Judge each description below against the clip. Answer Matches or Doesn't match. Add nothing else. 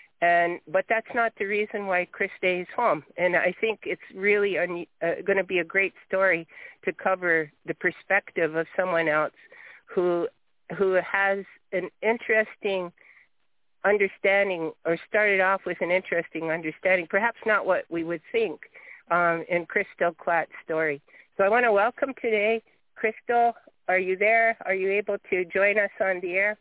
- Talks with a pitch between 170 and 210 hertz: Matches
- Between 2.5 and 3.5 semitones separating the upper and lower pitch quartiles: Matches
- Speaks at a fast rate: Doesn't match